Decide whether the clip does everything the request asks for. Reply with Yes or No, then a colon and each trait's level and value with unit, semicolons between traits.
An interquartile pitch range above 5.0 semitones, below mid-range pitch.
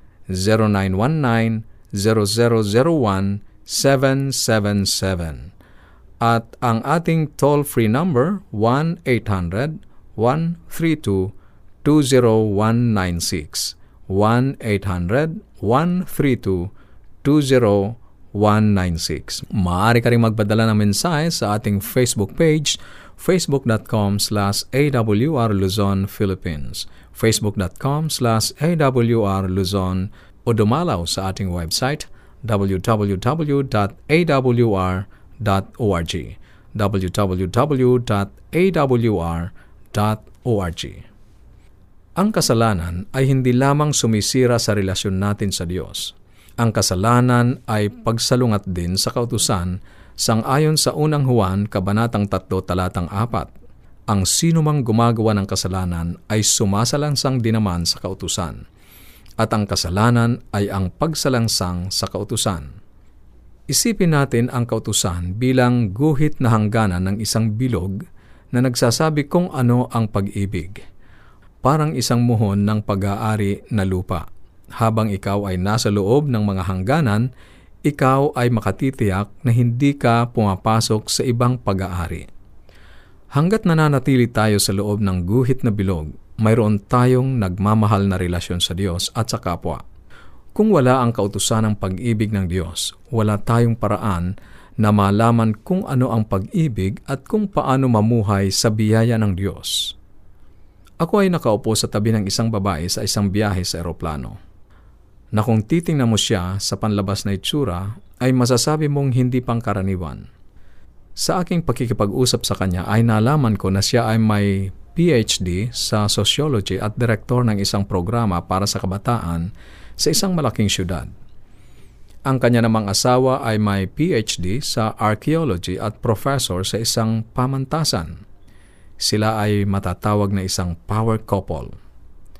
No: average, 4.3 semitones; low, 110 Hz